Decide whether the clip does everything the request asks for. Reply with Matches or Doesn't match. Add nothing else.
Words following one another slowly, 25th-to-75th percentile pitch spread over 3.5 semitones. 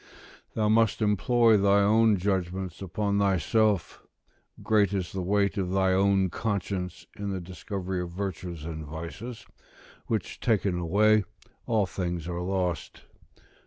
Doesn't match